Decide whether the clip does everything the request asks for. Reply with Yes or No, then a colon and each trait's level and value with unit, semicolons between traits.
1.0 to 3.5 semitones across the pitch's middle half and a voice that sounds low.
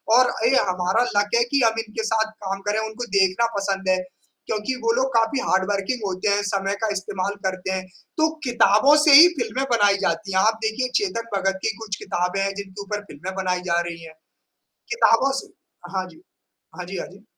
No: average, 3.2 semitones; high, 205 Hz